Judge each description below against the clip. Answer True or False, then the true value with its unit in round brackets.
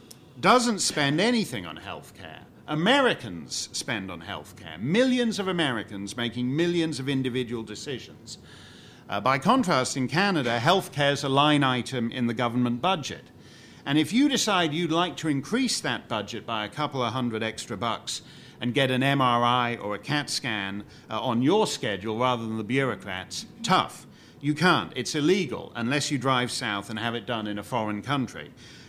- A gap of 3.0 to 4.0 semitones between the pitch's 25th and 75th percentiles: False (4.6 semitones)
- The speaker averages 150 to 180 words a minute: True (175 wpm)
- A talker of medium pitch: False (130 Hz)